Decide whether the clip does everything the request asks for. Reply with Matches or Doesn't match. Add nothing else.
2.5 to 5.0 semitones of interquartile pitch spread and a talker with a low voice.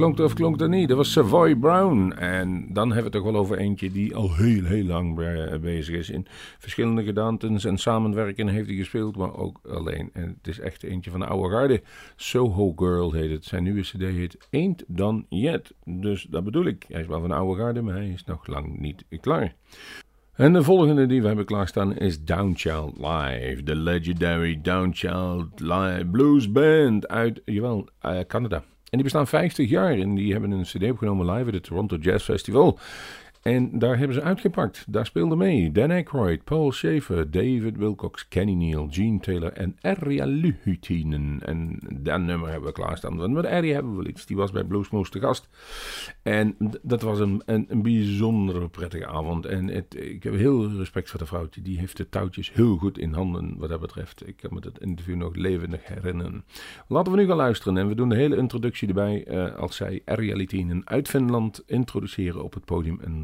Matches